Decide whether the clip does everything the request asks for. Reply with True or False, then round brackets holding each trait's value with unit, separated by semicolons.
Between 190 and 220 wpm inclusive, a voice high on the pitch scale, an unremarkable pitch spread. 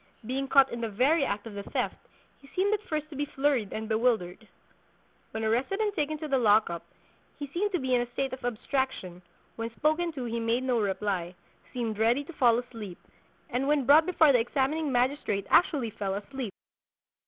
True (200 wpm; 250 Hz; 4.6 semitones)